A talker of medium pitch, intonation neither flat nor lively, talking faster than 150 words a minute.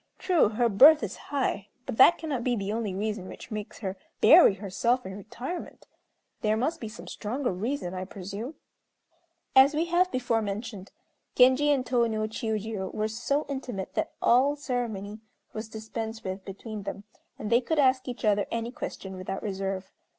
No: high, 220 Hz; average, 4.2 semitones; average, 170 wpm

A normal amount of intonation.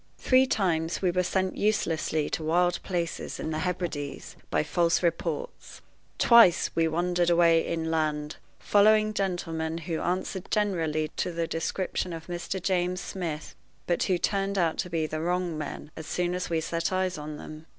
No: narrow, 2.3 semitones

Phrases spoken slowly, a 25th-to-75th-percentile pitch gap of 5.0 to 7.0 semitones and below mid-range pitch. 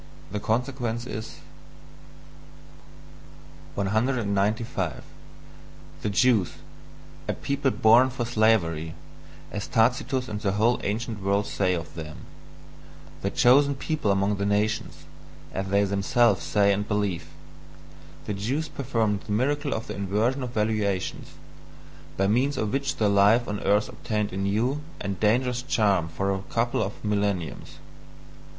No: slow, 130 wpm; average, 3.4 semitones; low, 105 Hz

